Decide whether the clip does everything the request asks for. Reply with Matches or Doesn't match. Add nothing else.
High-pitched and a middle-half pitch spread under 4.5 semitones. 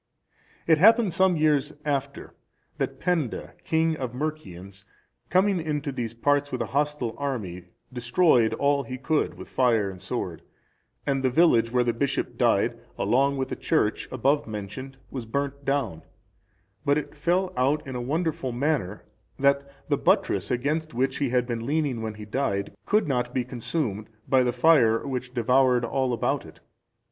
Doesn't match